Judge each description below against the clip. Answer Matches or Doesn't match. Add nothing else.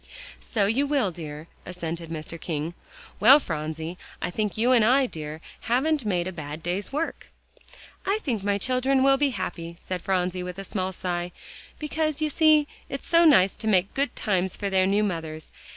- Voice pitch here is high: Matches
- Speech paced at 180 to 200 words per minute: Matches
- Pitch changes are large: Matches